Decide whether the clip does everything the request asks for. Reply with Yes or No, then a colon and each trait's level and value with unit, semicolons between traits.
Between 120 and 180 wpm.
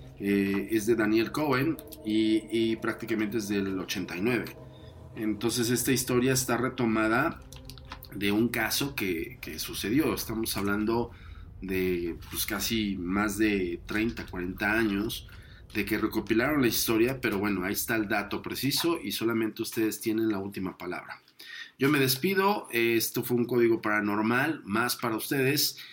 Yes: average, 145 wpm